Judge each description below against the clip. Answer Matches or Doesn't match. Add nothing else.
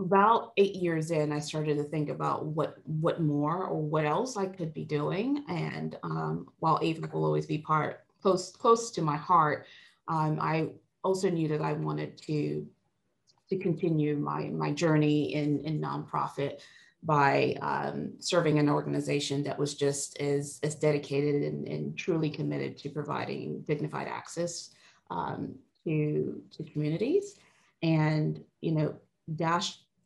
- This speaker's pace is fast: Doesn't match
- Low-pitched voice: Doesn't match